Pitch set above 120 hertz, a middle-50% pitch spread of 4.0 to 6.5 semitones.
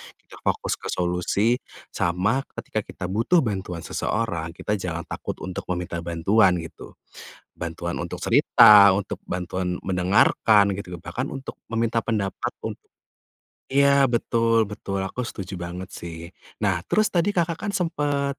No: low, 100 Hz; average, 4.8 semitones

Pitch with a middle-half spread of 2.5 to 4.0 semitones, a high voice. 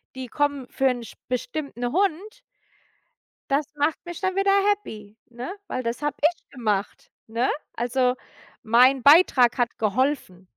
No: average, 4.5 semitones; very high, 260 Hz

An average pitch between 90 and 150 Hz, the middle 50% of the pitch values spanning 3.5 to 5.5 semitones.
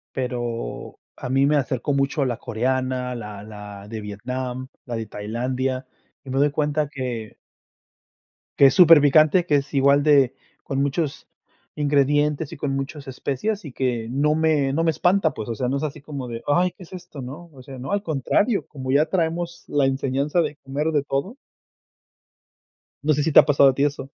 No: medium, 140 Hz; average, 2.9 semitones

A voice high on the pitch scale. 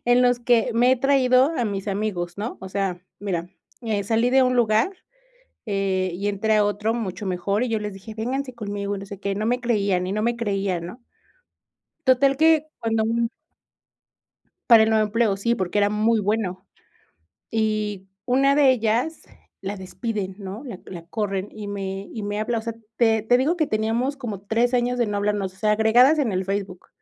Yes: high, 215 Hz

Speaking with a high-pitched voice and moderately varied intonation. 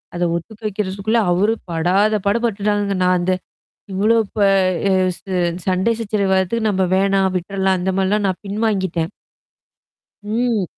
No: high, 195 Hz; narrow, 2.2 semitones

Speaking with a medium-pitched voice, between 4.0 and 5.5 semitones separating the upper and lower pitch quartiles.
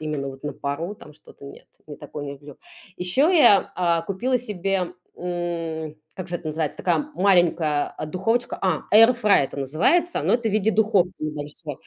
Yes: medium, 175 Hz; average, 5.0 semitones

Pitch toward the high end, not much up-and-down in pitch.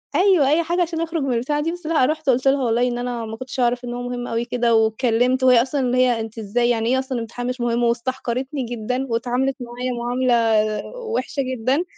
Yes: very high, 250 Hz; narrow, 2.2 semitones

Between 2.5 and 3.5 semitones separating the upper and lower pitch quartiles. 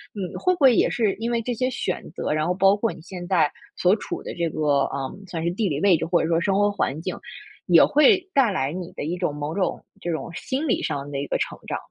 No: average, 5.2 semitones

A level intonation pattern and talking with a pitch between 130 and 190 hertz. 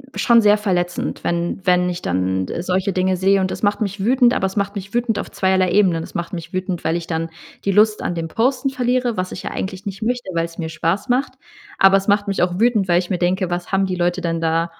No: average, 3.0 semitones; medium, 185 Hz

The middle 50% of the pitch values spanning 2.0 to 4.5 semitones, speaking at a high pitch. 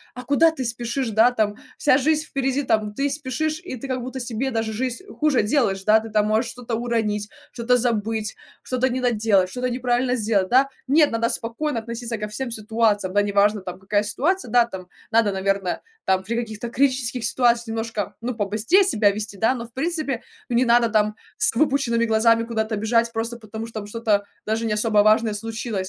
Yes: average, 2.8 semitones; high, 230 Hz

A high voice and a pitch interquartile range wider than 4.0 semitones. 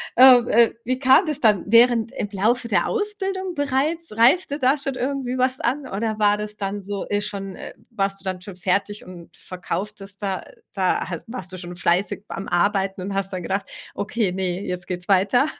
Yes: high, 205 Hz; average, 5.0 semitones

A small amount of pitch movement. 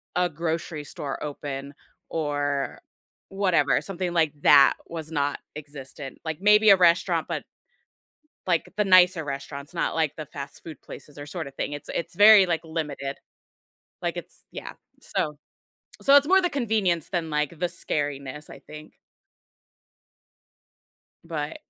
No: average, 3.7 semitones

